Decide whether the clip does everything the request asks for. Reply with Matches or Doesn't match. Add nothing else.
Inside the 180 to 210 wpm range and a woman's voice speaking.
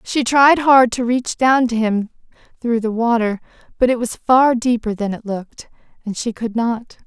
Matches